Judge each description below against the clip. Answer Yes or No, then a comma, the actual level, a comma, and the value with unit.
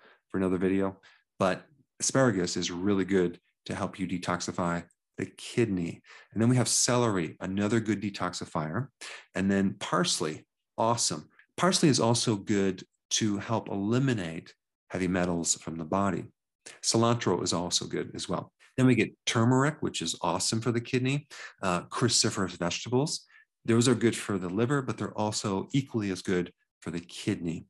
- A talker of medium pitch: No, low, 100 Hz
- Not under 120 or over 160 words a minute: Yes, average, 155 wpm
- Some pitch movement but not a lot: Yes, average, 4.5 semitones